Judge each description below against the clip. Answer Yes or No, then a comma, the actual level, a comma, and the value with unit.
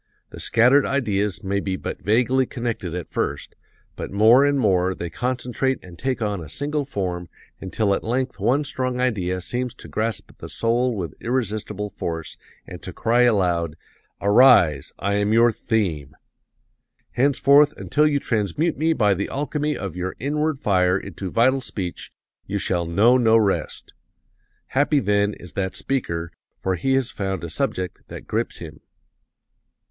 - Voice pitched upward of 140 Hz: No, low, 110 Hz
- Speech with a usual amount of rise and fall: No, wide, 5.7 semitones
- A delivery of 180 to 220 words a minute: No, average, 160 wpm